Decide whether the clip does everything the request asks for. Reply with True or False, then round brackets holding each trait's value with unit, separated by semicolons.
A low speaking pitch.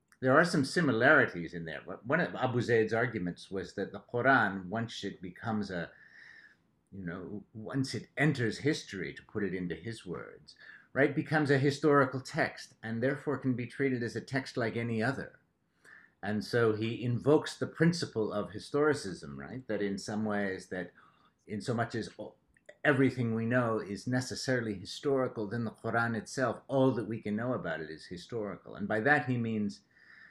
True (115 Hz)